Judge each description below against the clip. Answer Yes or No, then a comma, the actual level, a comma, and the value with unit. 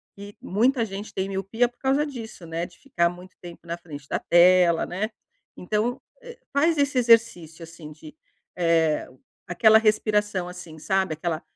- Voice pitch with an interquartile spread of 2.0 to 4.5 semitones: No, average, 4.9 semitones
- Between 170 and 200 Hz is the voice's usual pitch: Yes, high, 190 Hz